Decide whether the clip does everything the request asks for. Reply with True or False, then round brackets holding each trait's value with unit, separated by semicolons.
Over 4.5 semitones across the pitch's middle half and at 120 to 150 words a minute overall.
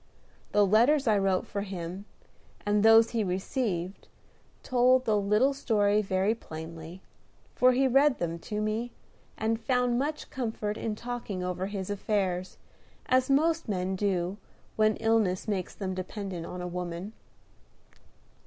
False (4.1 semitones; 140 wpm)